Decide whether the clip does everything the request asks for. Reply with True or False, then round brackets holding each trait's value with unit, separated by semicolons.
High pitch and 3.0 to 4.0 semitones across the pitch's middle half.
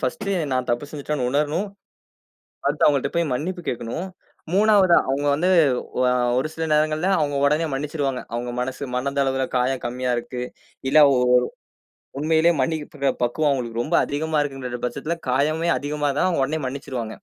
False (145 Hz; 3.6 semitones)